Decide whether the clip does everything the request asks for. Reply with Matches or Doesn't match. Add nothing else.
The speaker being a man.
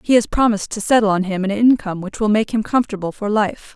Doesn't match